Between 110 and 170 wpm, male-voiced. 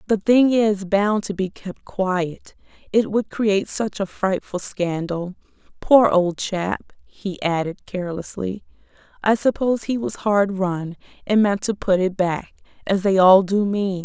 No: average, 155 wpm; female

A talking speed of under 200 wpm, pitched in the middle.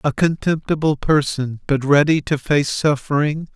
Yes: slow, 135 wpm; medium, 145 Hz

